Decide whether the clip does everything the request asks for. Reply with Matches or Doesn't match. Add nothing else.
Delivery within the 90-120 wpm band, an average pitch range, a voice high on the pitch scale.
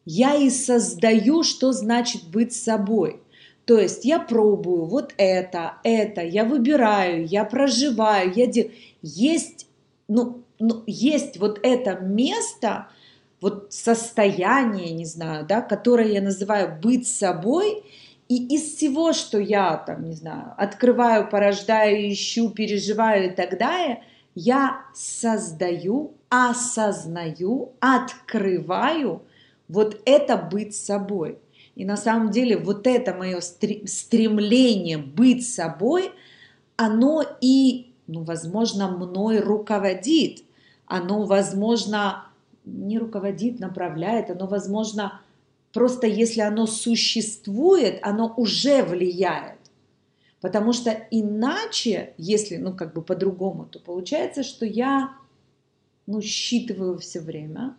Matches